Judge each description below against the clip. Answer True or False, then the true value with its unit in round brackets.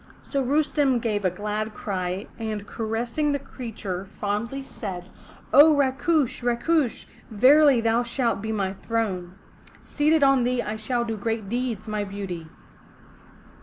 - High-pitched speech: True (230 Hz)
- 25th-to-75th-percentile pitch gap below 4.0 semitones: False (4.3 semitones)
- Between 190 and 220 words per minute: False (135 wpm)